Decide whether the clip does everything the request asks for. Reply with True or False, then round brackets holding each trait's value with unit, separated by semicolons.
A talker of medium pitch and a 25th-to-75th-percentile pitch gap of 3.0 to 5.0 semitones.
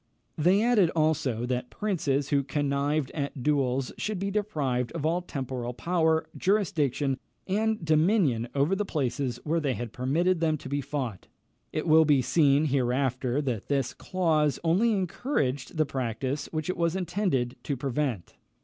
True (145 Hz; 4.6 semitones)